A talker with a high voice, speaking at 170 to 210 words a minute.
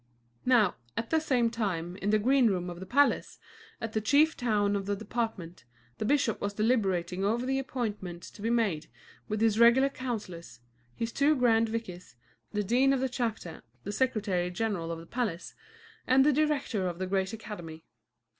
Yes: high, 220 Hz; average, 180 wpm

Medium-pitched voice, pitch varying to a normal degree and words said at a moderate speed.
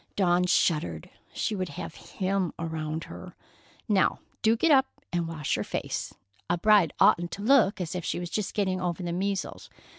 Yes: medium, 180 Hz; average, 3.2 semitones; average, 180 wpm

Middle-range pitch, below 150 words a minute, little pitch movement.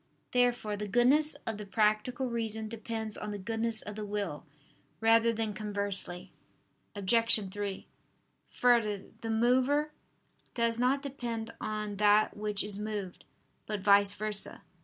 No: high, 215 Hz; slow, 135 wpm; narrow, 2.2 semitones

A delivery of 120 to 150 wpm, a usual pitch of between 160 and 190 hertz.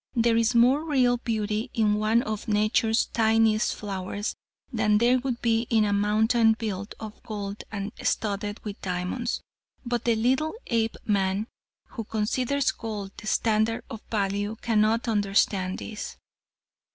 No: average, 140 wpm; high, 220 Hz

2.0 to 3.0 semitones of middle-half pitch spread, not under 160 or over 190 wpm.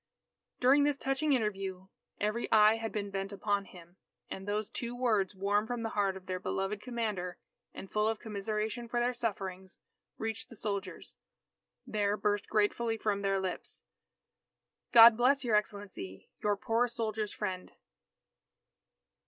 No: average, 2.7 semitones; average, 150 wpm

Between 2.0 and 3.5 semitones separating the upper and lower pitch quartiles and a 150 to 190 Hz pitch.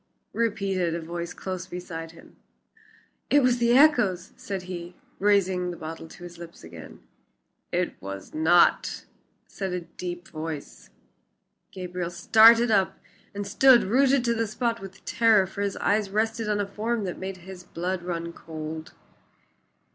No: average, 4.1 semitones; medium, 185 Hz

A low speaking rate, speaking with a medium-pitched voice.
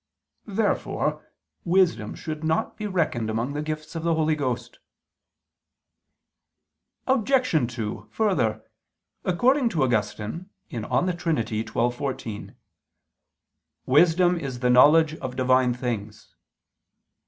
Yes: slow, 105 wpm; medium, 150 Hz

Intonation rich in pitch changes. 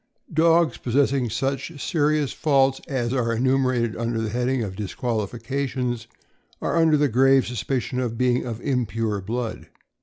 No: average, 2.9 semitones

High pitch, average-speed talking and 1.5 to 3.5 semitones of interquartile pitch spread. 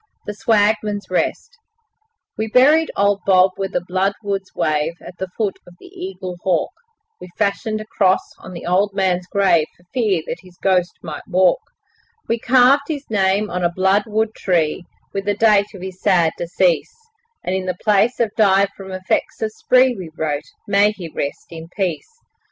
Yes: high, 195 Hz; average, 170 wpm; average, 2.9 semitones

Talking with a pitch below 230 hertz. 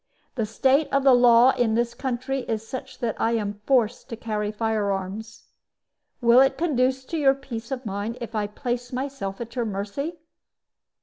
No: high, 235 Hz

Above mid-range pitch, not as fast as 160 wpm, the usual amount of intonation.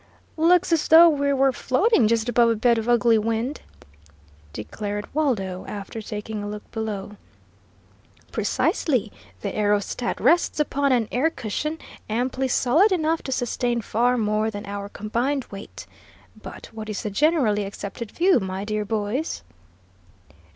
Yes: high, 230 Hz; average, 145 wpm; average, 4.8 semitones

